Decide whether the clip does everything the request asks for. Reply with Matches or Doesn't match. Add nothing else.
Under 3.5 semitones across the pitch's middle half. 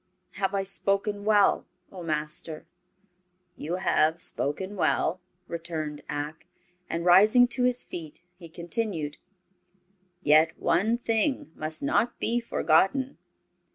Doesn't match